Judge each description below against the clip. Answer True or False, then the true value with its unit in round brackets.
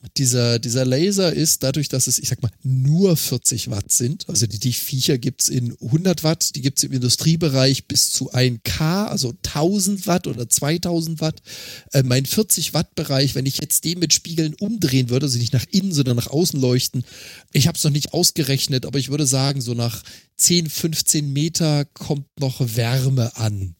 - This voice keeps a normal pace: False (195 wpm)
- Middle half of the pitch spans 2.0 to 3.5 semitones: False (4.2 semitones)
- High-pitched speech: False (140 Hz)